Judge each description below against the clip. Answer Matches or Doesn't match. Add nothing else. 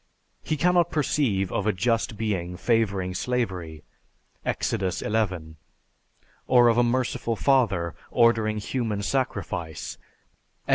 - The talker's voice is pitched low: Matches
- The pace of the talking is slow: Matches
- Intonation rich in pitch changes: Doesn't match